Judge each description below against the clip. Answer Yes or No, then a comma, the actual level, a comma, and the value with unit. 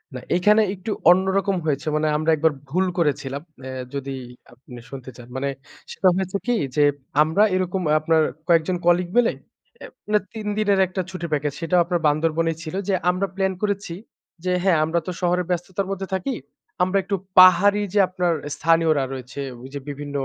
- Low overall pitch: No, medium, 175 Hz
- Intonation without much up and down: No, average, 3.9 semitones